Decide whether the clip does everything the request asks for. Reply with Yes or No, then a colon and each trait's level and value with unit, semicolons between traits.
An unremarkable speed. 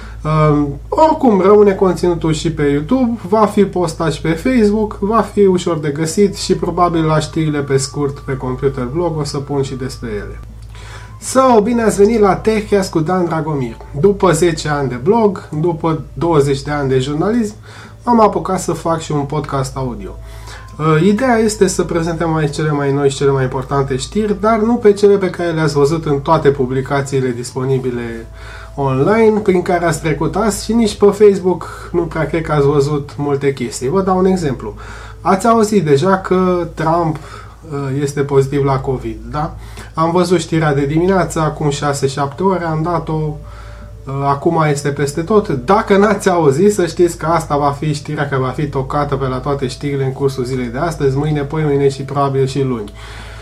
No: fast, 185 wpm